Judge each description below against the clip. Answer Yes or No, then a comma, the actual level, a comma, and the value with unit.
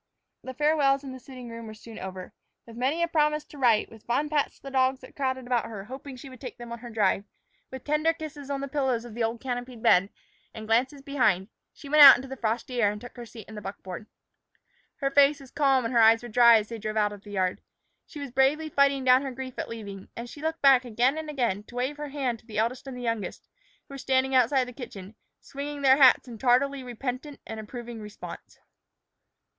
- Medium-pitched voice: No, very high, 250 Hz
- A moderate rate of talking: No, fast, 240 wpm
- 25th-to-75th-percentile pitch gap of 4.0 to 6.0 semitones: No, average, 3.4 semitones